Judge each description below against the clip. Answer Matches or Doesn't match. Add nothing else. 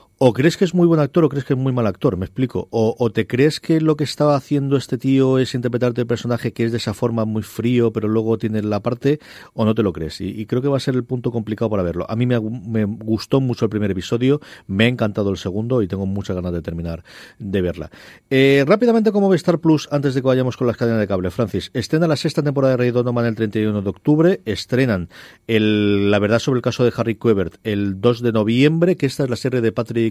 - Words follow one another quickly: Matches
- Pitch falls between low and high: Doesn't match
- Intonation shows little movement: Doesn't match